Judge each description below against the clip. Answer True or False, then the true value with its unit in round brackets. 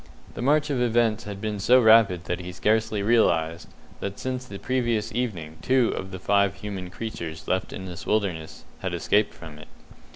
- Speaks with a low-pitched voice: True (100 Hz)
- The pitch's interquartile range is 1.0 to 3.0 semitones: False (4.3 semitones)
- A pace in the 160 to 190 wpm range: True (185 wpm)